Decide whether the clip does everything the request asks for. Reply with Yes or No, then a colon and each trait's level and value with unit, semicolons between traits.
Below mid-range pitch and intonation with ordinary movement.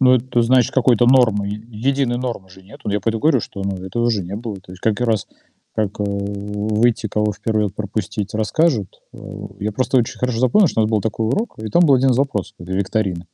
Yes: low, 110 Hz; average, 3.3 semitones